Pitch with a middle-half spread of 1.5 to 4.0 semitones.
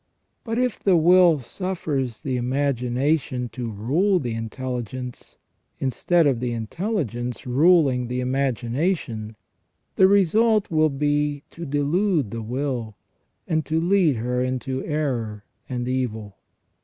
No: average, 5.1 semitones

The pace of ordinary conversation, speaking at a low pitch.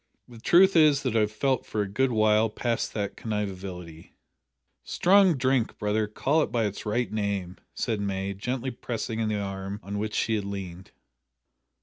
Yes: average, 175 wpm; low, 110 Hz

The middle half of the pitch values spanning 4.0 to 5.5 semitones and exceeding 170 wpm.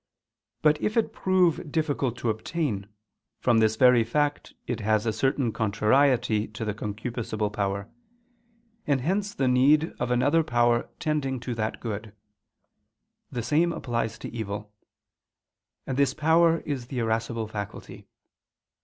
No: average, 4.9 semitones; slow, 135 wpm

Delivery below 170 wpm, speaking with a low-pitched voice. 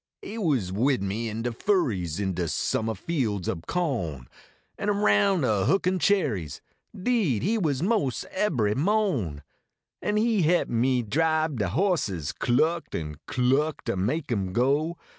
Yes: average, 160 wpm; low, 130 Hz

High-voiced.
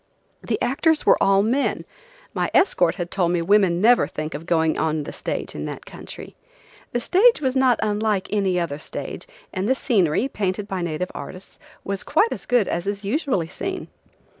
Yes: high, 200 Hz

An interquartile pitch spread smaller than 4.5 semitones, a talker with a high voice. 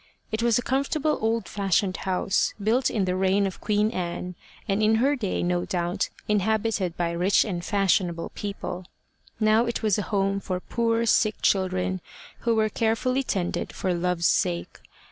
Yes: average, 3.5 semitones; high, 200 Hz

